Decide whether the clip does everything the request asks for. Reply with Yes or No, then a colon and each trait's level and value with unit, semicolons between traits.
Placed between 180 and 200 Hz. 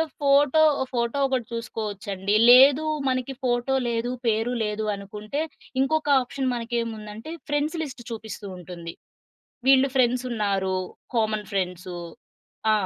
No: high, 235 Hz